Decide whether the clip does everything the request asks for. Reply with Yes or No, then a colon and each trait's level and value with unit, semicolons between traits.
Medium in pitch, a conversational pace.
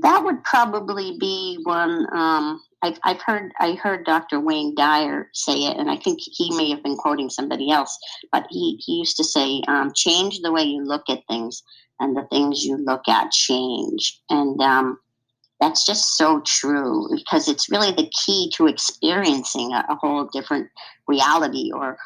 Yes: medium, 155 Hz; average, 180 wpm